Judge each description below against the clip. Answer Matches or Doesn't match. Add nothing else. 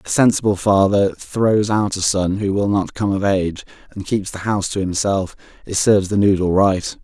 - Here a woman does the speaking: Doesn't match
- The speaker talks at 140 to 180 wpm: Doesn't match